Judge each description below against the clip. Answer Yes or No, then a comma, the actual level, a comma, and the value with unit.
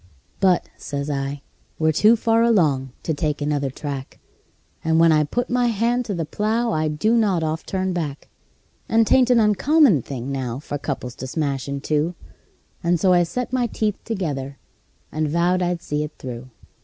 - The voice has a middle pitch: Yes, medium, 160 Hz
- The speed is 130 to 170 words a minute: No, average, 180 wpm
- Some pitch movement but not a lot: No, wide, 6.8 semitones